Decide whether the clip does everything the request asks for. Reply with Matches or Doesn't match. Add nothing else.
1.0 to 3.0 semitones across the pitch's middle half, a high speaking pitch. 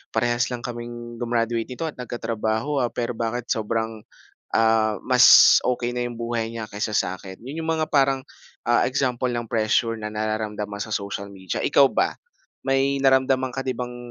Doesn't match